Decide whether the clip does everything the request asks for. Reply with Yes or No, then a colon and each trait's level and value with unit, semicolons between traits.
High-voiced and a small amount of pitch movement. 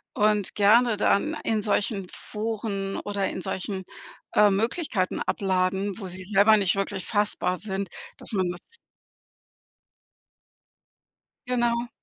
Yes: high, 200 Hz; narrow, 2.3 semitones